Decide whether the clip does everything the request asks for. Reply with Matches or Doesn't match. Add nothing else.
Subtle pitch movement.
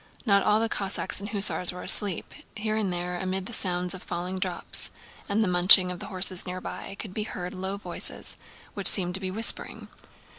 Matches